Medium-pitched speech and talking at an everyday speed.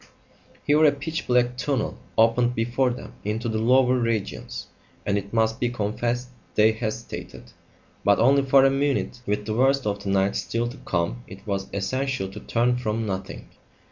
No: low, 115 Hz; average, 175 wpm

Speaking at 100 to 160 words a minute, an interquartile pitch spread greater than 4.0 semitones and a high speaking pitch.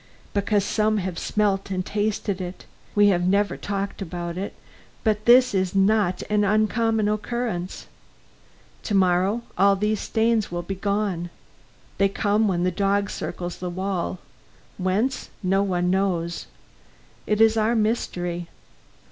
No: average, 140 wpm; narrow, 2.6 semitones; high, 200 Hz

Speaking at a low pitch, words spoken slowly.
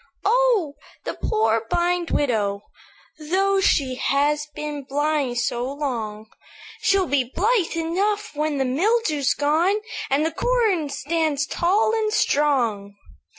No: very high, 300 Hz; slow, 120 wpm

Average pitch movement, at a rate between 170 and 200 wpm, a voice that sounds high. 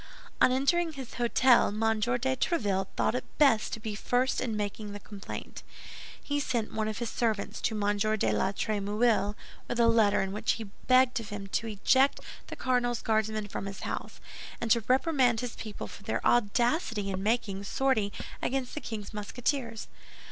Yes: average, 3.3 semitones; average, 175 wpm; high, 225 Hz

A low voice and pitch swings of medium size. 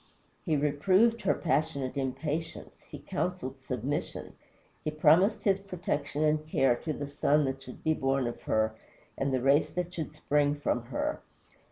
No: medium, 145 Hz; average, 3.1 semitones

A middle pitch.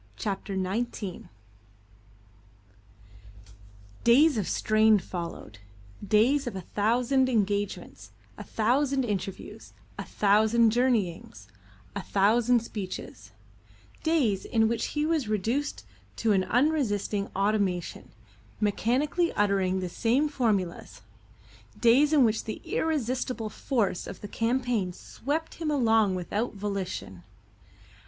No: high, 220 Hz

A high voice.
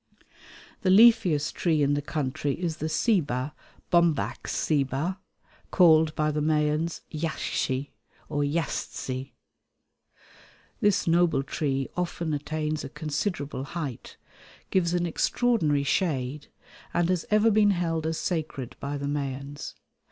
No: medium, 155 Hz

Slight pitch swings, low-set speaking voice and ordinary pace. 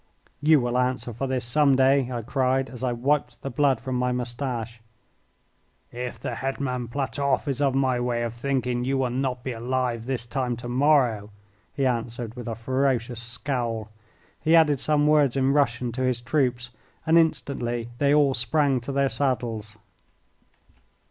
Yes: narrow, 2.3 semitones; low, 125 Hz; average, 170 wpm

